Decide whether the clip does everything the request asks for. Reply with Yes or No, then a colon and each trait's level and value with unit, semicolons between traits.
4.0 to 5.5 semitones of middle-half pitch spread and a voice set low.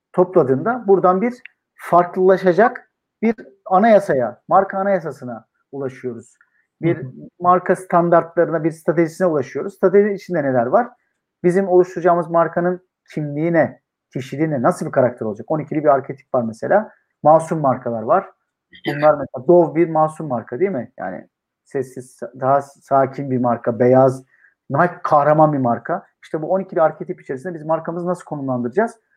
No: average, 5.0 semitones; medium, 165 Hz